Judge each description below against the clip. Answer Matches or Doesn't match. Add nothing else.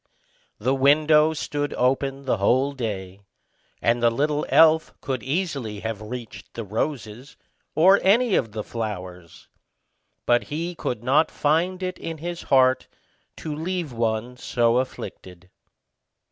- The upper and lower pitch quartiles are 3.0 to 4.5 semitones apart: Doesn't match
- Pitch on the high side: Doesn't match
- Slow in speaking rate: Matches